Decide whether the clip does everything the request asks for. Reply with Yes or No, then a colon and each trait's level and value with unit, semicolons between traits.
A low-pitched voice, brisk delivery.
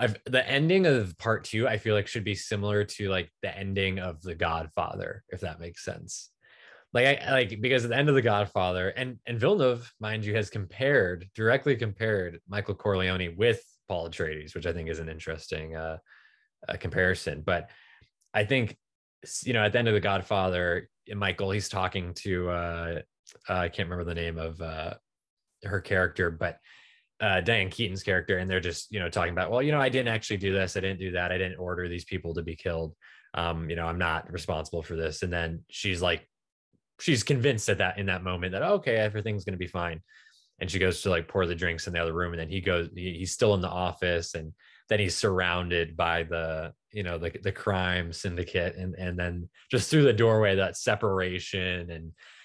Yes: very low, 95 Hz; fast, 210 wpm